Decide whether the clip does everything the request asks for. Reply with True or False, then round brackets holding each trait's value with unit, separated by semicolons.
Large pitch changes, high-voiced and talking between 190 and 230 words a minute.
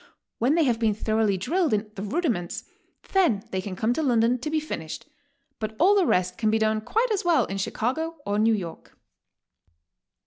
True (7.4 semitones; 225 Hz; 195 wpm)